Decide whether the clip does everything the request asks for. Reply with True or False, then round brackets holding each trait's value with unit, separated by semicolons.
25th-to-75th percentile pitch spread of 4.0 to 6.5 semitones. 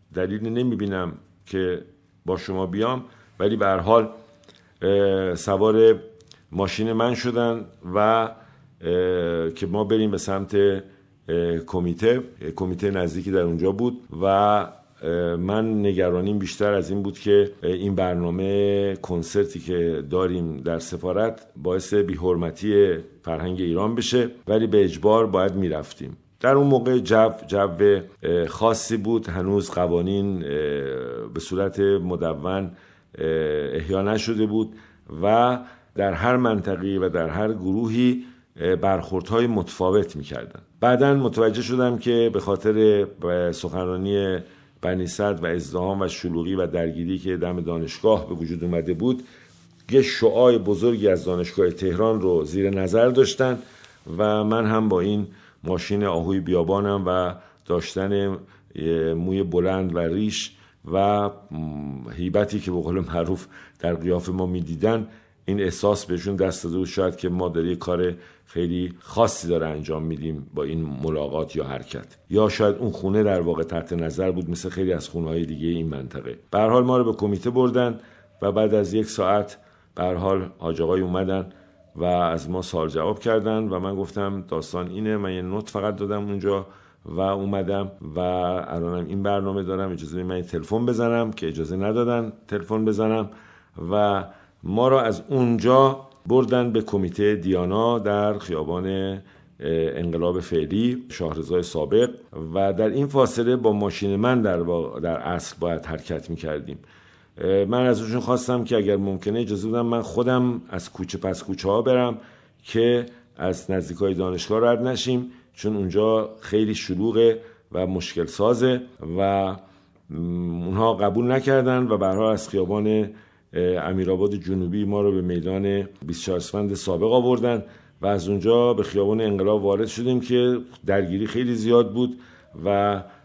False (3.6 semitones)